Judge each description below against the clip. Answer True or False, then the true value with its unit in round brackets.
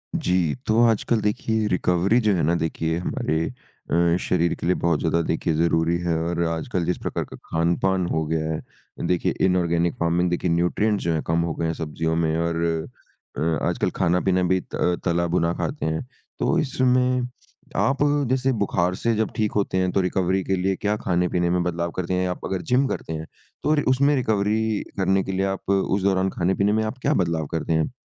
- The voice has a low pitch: True (90 Hz)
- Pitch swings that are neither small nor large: True (3.4 semitones)